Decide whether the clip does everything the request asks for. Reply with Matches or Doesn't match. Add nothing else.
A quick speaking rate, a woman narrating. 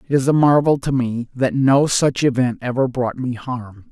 Doesn't match